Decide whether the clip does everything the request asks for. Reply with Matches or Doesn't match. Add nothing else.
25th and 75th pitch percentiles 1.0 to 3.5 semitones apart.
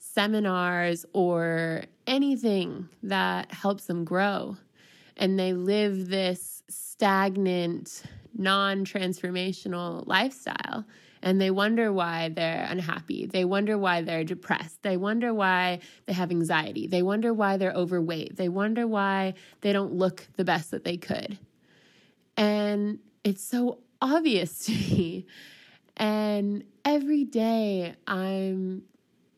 Matches